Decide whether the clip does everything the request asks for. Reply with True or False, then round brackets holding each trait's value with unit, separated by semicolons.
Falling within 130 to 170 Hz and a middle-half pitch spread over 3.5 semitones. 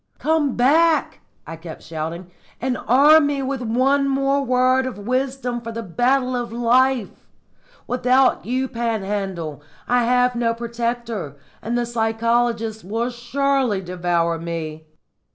False (240 Hz; 3.9 semitones)